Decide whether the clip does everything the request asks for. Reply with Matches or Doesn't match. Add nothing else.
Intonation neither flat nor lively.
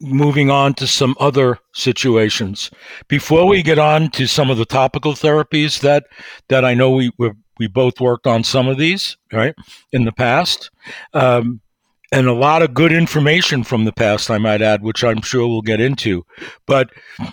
Matches